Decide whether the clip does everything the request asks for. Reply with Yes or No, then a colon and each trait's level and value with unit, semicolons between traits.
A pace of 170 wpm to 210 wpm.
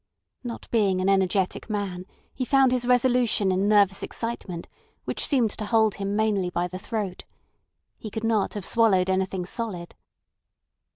No: average, 155 wpm